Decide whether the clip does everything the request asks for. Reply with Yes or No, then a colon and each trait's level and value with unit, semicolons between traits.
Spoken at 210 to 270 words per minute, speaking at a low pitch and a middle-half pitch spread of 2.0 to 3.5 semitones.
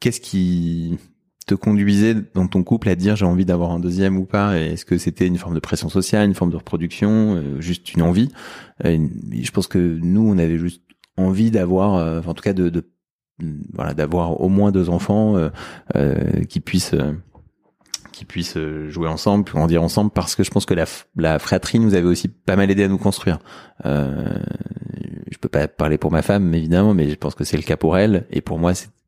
Yes: average, 215 wpm; very low, 90 Hz; average, 3.0 semitones